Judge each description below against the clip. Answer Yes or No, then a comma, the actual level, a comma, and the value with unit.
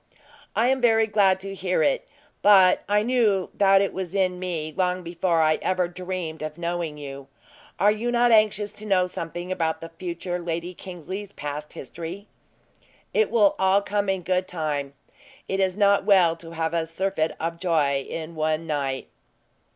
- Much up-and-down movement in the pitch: No, average, 3.2 semitones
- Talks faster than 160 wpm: Yes, average, 175 wpm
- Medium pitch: Yes, medium, 180 Hz